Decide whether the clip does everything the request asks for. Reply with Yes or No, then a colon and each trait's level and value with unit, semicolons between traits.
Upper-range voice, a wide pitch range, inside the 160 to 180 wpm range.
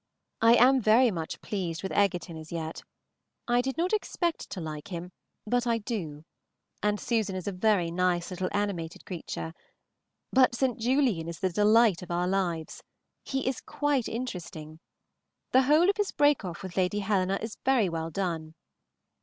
Yes: high, 195 Hz; wide, 6.0 semitones; average, 170 wpm